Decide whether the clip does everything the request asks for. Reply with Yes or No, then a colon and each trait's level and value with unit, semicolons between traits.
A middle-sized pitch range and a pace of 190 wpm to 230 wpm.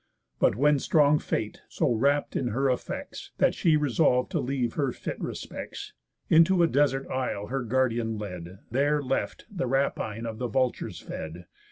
No: average, 4.0 semitones; average, 165 wpm